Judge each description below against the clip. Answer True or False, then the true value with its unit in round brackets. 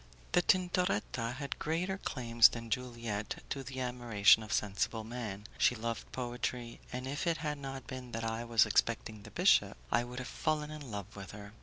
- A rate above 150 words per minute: True (185 wpm)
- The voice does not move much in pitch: False (3.3 semitones)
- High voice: False (120 Hz)